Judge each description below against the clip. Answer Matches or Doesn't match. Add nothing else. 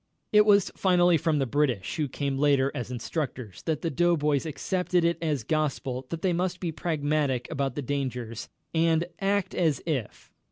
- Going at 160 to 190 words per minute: Matches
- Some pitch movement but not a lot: Matches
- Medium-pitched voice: Matches